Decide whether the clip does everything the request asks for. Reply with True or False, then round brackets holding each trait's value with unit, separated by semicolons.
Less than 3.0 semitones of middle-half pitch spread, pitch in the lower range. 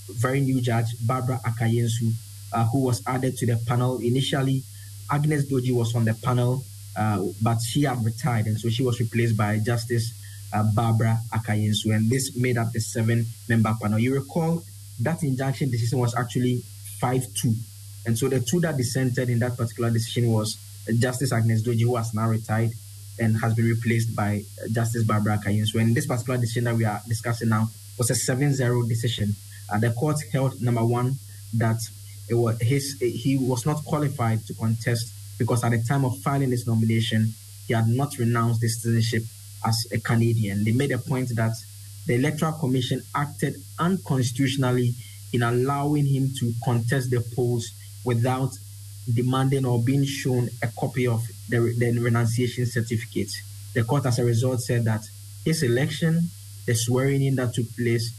True (2.4 semitones; 115 Hz)